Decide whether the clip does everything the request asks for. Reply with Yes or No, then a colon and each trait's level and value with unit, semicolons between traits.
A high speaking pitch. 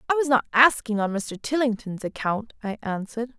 Yes: high, 235 Hz